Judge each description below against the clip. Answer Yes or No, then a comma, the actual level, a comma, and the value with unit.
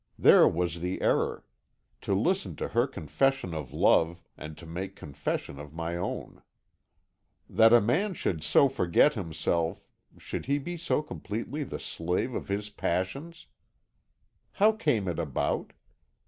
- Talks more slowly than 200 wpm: Yes, average, 140 wpm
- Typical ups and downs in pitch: No, wide, 8.4 semitones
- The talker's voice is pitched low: Yes, very low, 95 Hz